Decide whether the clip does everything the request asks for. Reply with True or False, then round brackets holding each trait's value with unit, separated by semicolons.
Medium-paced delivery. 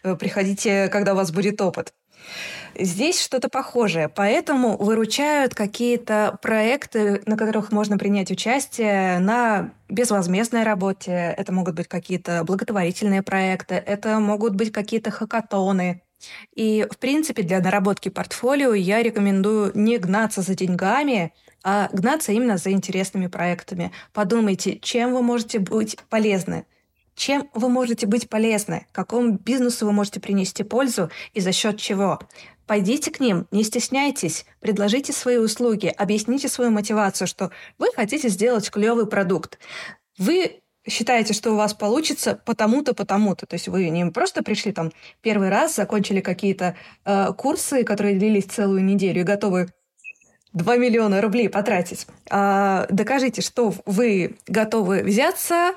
True (135 wpm)